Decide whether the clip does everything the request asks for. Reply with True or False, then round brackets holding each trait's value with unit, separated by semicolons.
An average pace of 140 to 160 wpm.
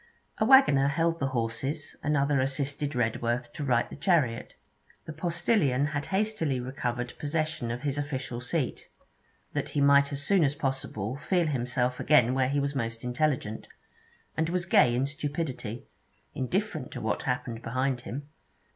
True (155 wpm)